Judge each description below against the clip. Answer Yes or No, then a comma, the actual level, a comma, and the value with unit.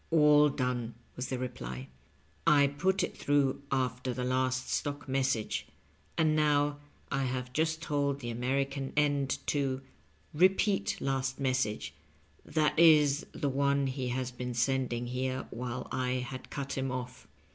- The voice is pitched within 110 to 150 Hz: Yes, low, 135 Hz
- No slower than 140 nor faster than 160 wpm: Yes, average, 155 wpm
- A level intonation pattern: Yes, narrow, 2.3 semitones